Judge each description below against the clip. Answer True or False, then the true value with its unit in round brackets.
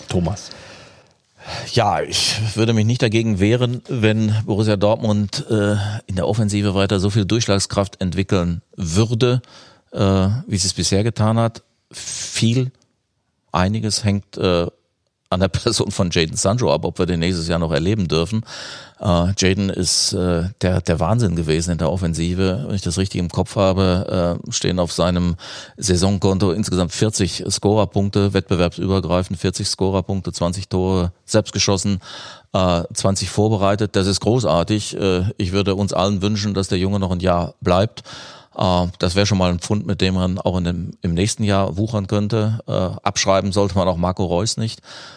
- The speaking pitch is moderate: False (100 Hz)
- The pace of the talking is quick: False (165 wpm)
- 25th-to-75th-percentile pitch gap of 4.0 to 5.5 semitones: False (2.8 semitones)